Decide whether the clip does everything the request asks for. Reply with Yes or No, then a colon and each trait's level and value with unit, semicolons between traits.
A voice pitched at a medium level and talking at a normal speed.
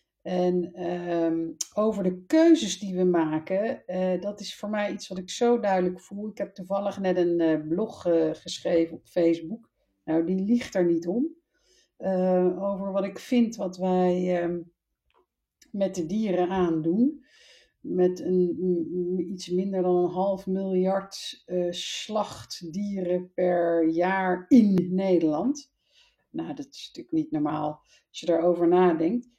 Yes: medium, 180 Hz; average, 150 wpm